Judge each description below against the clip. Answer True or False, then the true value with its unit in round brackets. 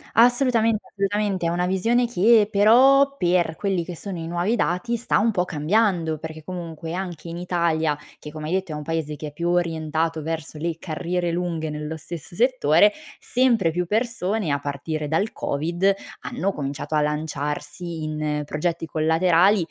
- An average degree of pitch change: True (4.1 semitones)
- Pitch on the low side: False (170 Hz)